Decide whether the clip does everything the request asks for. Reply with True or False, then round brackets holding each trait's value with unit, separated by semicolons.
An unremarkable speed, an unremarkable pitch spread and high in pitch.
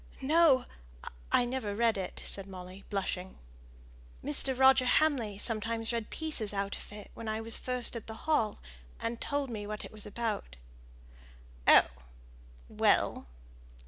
True (145 wpm; 3.7 semitones; 225 Hz)